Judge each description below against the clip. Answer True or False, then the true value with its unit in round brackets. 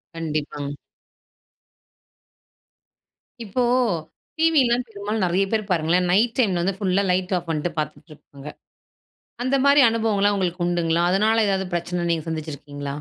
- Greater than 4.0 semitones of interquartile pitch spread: True (4.6 semitones)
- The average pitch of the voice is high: False (180 Hz)